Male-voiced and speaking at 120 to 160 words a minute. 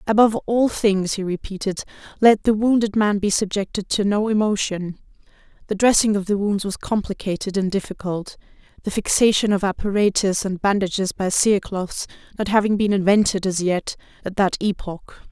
No: female; average, 155 wpm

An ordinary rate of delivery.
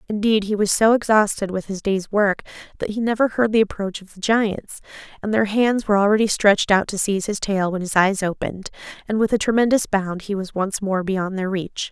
No: fast, 225 wpm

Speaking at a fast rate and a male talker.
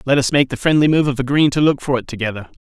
Yes: fast, 295 wpm; male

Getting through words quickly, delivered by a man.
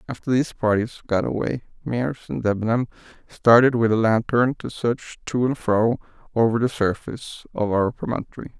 No: average, 160 wpm; male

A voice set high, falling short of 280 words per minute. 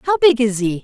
No: very high, 250 Hz; fast, 285 wpm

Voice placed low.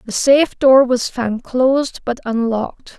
No: very high, 250 Hz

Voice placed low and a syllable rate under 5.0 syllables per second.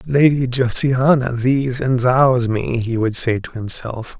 Yes: low, 125 Hz; 3.7 syllables/s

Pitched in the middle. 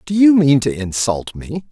Yes: medium, 145 Hz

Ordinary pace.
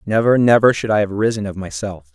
No: fast, 225 wpm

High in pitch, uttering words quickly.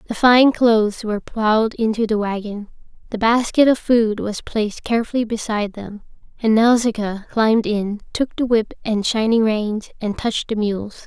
No: high, 220 Hz; average, 170 wpm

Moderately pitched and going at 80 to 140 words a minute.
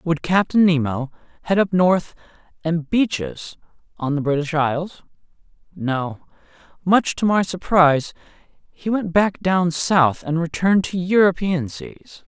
Yes: medium, 165 Hz; slow, 135 wpm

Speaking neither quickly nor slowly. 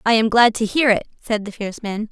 No: fast, 285 wpm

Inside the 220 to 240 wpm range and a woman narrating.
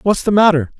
No: fast, 230 wpm; male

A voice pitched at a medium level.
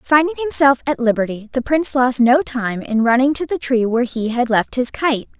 No: very high, 260 Hz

